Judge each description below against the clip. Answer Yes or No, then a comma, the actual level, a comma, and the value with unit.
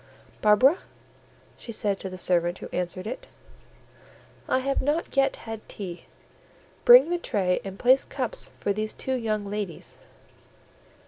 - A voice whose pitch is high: Yes, high, 215 Hz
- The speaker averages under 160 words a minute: Yes, average, 140 wpm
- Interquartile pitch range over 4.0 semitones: Yes, average, 5.3 semitones